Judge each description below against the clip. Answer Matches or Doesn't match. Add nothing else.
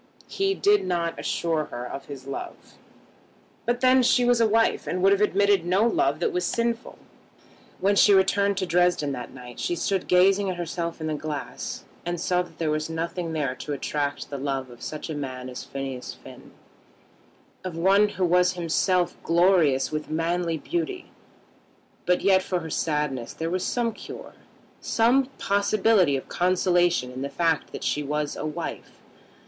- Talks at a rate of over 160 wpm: Matches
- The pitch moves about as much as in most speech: Matches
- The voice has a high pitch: Doesn't match